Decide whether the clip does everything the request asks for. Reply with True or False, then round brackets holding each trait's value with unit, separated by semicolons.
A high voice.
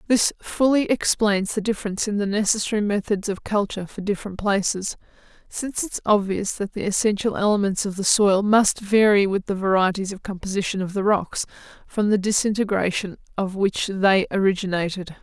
True (200 Hz)